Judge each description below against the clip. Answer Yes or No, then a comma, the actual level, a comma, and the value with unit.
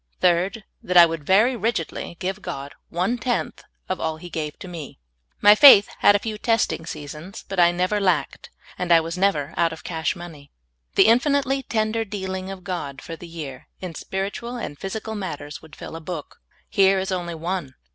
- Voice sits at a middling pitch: Yes, medium, 180 Hz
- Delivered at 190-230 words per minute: Yes, average, 195 wpm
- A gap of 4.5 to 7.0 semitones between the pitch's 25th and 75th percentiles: No, average, 4.0 semitones